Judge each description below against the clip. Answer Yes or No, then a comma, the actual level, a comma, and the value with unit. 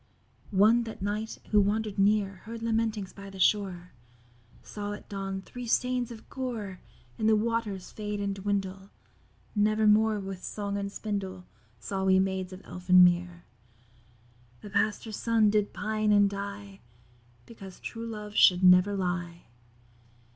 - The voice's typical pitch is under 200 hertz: No, high, 205 Hz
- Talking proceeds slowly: No, average, 145 wpm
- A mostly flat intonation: Yes, narrow, 2.0 semitones